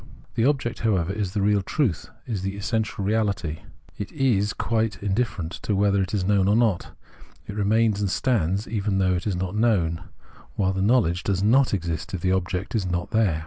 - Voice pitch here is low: Yes, low, 100 Hz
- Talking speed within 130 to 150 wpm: No, average, 195 wpm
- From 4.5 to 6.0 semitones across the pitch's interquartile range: No, average, 3.0 semitones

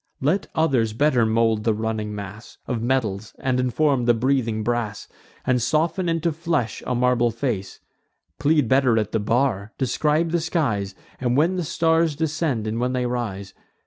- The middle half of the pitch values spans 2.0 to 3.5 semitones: No, average, 5.2 semitones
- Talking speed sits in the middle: Yes, average, 165 wpm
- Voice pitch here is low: Yes, low, 125 Hz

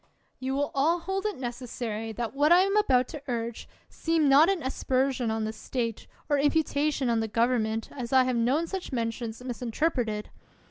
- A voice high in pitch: Yes, very high, 255 Hz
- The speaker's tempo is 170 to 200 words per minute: Yes, average, 180 wpm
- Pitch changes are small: No, average, 4.3 semitones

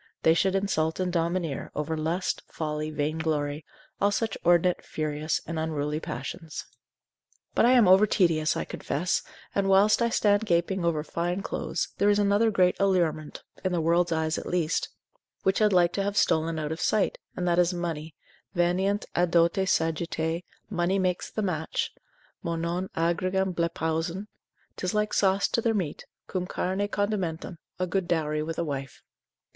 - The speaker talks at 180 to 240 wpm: No, average, 165 wpm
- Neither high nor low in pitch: Yes, medium, 175 Hz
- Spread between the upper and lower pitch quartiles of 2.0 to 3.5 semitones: Yes, average, 3.1 semitones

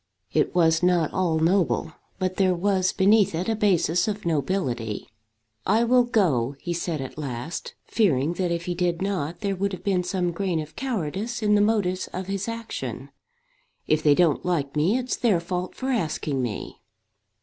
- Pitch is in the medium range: Yes, medium, 180 Hz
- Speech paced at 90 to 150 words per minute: No, average, 180 wpm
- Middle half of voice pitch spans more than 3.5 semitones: Yes, average, 3.9 semitones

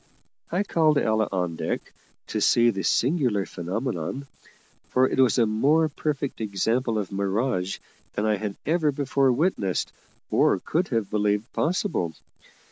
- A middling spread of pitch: No, wide, 5.8 semitones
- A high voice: No, low, 115 Hz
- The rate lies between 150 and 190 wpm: No, average, 140 wpm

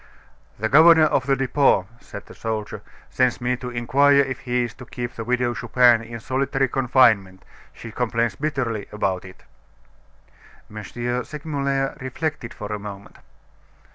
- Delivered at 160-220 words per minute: No, average, 145 wpm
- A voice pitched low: Yes, low, 125 Hz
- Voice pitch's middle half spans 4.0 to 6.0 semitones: No, average, 3.3 semitones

